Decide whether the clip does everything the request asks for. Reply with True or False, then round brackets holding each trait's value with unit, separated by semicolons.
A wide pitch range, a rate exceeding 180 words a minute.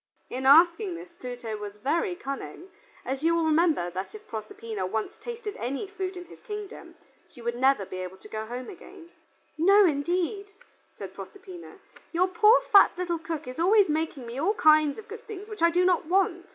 True (7.2 semitones; 190 wpm)